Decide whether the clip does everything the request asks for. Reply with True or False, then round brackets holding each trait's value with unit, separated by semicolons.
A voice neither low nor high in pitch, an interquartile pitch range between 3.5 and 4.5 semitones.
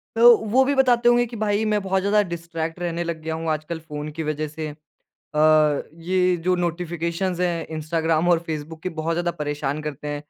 False (170 Hz; 3.1 semitones)